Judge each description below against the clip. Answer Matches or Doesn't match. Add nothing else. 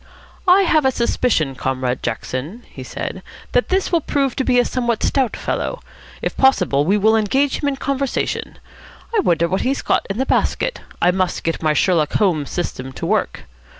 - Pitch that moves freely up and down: Matches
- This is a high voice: Matches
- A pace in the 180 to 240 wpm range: Matches